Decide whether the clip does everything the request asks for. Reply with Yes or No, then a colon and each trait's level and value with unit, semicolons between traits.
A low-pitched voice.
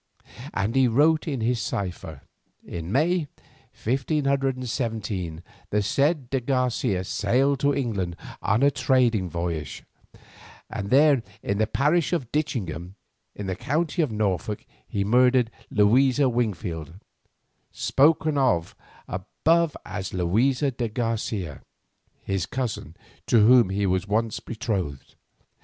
Yes: low, 115 Hz